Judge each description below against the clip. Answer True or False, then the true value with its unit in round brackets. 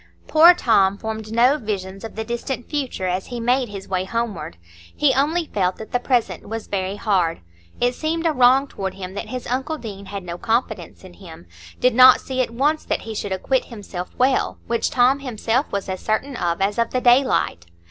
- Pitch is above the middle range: True (230 Hz)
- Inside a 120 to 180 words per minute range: False (200 wpm)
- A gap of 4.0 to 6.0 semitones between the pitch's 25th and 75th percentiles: True (4.9 semitones)